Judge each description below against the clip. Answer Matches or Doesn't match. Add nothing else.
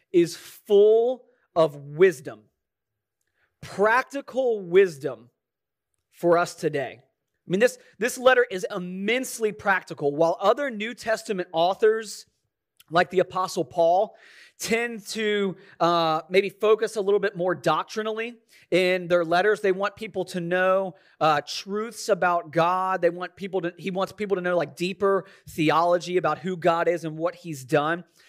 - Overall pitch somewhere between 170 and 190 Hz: Matches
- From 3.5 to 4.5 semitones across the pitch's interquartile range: Matches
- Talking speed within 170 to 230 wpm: Doesn't match